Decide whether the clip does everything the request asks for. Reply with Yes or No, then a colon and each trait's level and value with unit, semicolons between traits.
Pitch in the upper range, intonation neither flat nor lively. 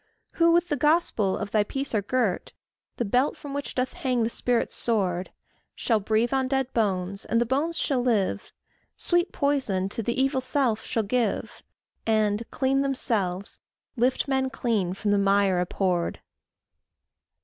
Yes: high, 235 Hz; average, 4.8 semitones